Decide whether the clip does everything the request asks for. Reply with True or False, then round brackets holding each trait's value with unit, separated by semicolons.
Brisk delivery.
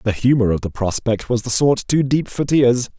True (240 wpm)